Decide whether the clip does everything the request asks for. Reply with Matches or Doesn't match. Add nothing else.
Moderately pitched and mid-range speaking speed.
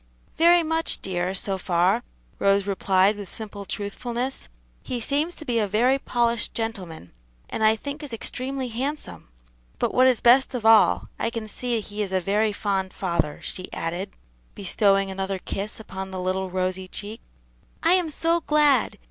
Doesn't match